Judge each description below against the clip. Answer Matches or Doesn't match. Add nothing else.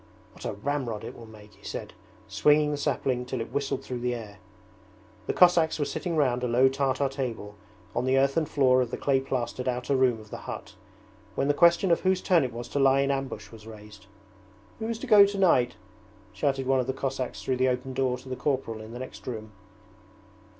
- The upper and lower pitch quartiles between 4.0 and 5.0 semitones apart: Doesn't match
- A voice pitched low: Matches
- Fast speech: Matches